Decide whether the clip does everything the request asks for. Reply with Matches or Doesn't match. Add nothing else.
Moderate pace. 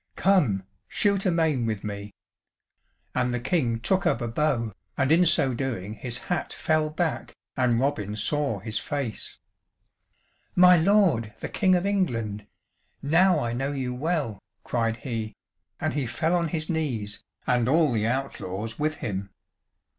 Matches